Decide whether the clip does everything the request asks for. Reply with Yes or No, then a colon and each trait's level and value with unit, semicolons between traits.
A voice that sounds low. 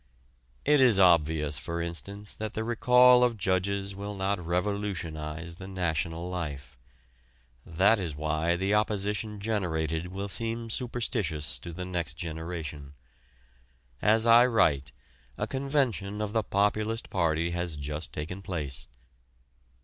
Yes: very low, 95 Hz